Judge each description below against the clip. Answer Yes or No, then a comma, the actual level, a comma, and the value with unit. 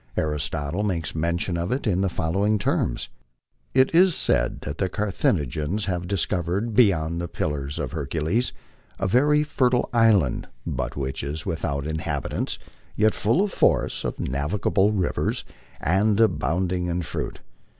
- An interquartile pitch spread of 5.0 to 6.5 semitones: Yes, wide, 5.5 semitones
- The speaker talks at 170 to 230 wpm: No, average, 145 wpm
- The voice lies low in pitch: Yes, very low, 90 Hz